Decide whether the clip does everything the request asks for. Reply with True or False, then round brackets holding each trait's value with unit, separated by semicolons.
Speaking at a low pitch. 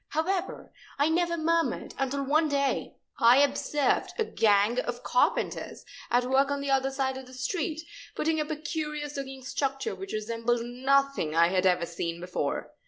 False (275 Hz)